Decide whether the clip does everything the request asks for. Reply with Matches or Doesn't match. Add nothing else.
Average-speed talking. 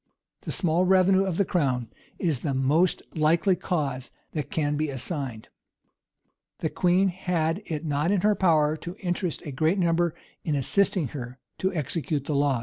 Matches